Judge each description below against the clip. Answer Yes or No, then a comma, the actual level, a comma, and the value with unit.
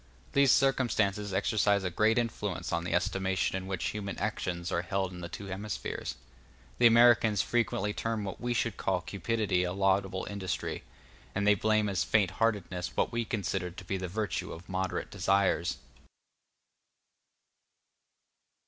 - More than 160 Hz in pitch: No, low, 100 Hz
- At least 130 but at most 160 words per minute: Yes, average, 150 wpm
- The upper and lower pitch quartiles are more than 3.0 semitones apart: No, narrow, 2.6 semitones